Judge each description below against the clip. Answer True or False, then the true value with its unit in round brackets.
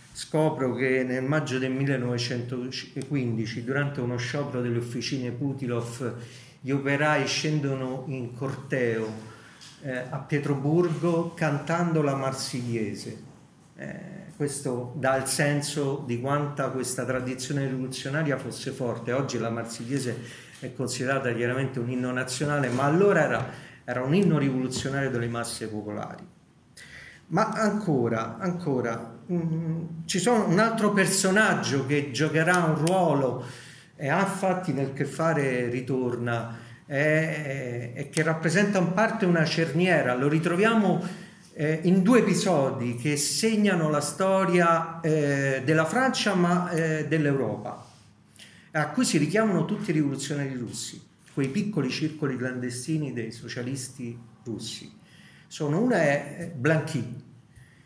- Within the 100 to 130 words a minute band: True (120 wpm)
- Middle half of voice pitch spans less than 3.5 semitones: False (4.5 semitones)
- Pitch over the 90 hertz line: True (140 Hz)